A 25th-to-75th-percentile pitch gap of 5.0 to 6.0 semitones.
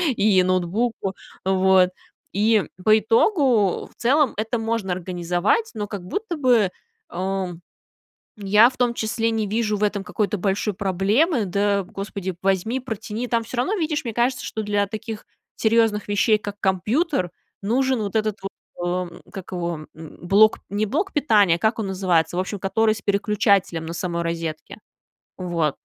No: average, 3.3 semitones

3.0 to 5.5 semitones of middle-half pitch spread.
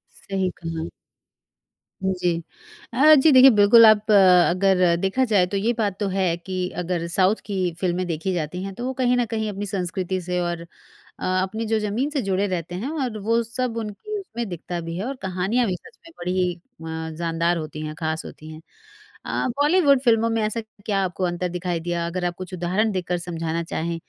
Yes: average, 4.0 semitones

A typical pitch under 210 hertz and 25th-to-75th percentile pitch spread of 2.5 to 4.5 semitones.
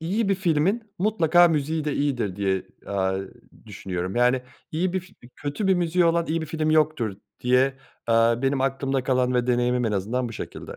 No: medium, 140 Hz; average, 5.3 semitones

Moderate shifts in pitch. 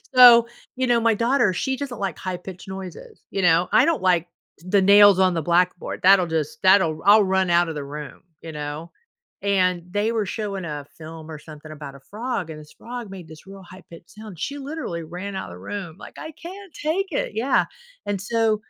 Yes: average, 5.0 semitones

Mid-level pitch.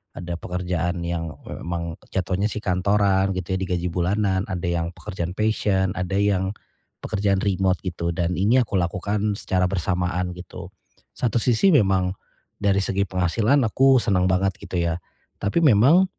No: very low, 95 Hz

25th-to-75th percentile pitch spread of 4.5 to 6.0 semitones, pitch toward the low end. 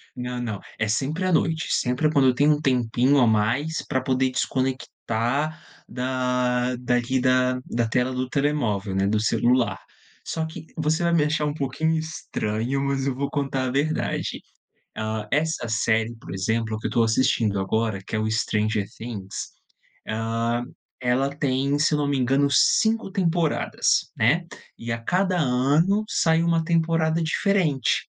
Yes: average, 4.8 semitones; low, 130 Hz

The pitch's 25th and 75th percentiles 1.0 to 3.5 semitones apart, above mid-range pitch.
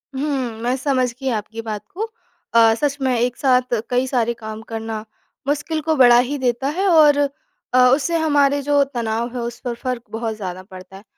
No: average, 4.0 semitones; very high, 250 Hz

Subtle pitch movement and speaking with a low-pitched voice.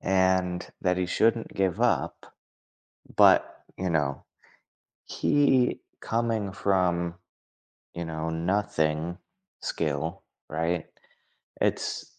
No: average, 3.1 semitones; very low, 90 Hz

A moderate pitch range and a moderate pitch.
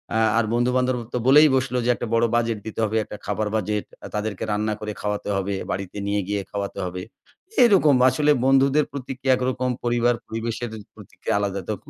No: average, 3.7 semitones; low, 115 Hz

